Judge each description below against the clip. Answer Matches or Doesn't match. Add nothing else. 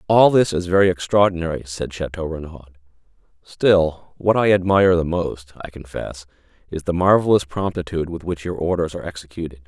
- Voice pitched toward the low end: Matches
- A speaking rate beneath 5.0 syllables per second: Doesn't match